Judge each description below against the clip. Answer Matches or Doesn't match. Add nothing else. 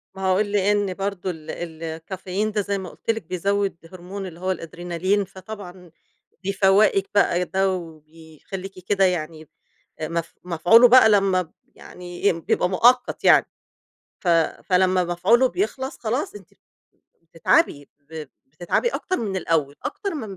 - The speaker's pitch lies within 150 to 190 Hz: Matches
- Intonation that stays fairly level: Doesn't match